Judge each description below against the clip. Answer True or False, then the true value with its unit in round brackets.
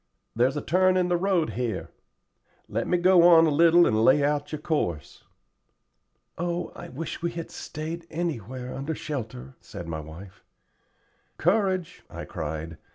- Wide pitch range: True (7.6 semitones)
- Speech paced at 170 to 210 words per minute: False (155 wpm)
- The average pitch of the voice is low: False (155 Hz)